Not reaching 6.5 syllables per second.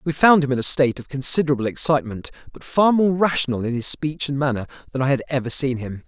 No: 6.6 syllables/s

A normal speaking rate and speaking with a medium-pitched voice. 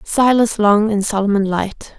No: average, 150 wpm; high, 210 Hz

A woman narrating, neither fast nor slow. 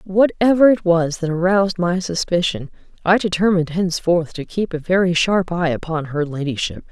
Yes: female; average, 165 wpm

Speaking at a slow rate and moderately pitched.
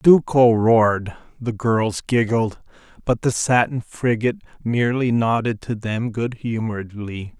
No: slow, 120 wpm; low, 115 Hz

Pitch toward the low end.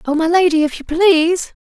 No: very high, 330 Hz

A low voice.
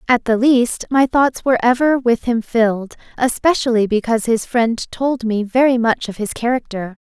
No: high, 240 Hz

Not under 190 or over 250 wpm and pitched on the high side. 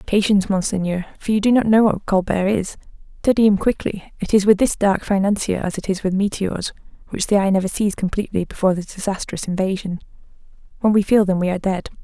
Yes: average, 200 wpm; high, 195 Hz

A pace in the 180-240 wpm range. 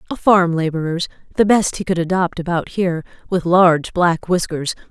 No: average, 170 wpm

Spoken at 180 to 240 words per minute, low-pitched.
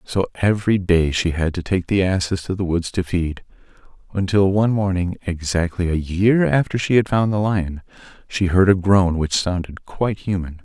Yes: average, 190 wpm; very low, 90 Hz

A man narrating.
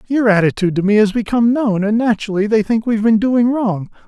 Yes: male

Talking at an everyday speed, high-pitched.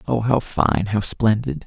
No: average, 180 wpm; low, 100 Hz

